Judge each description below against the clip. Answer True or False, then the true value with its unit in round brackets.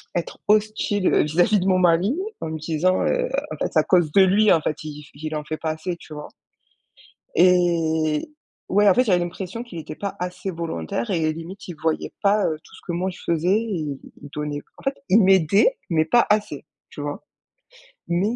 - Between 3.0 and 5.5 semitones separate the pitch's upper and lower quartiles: True (3.9 semitones)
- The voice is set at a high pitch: False (175 Hz)